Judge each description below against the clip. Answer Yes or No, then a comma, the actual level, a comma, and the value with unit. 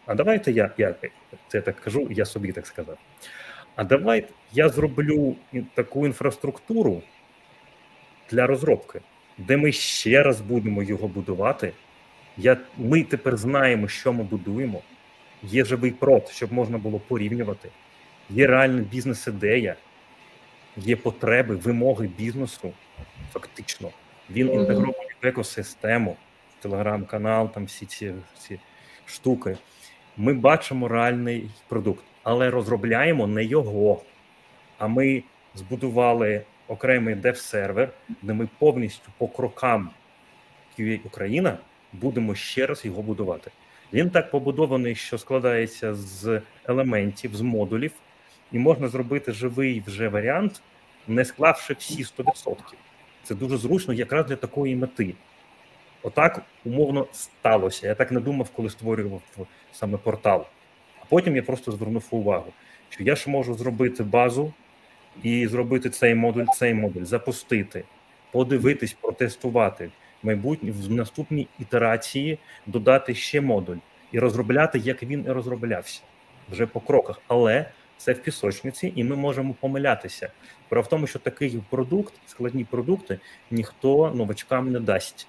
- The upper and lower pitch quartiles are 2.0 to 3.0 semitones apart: No, average, 3.4 semitones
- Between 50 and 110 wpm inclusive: No, average, 125 wpm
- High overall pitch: No, low, 125 Hz